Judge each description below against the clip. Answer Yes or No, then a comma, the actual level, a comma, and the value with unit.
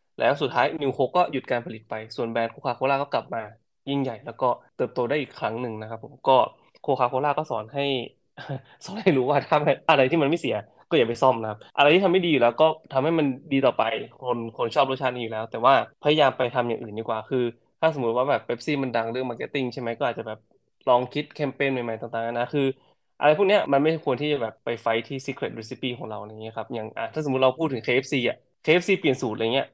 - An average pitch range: Yes, average, 3.8 semitones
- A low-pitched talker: Yes, low, 130 Hz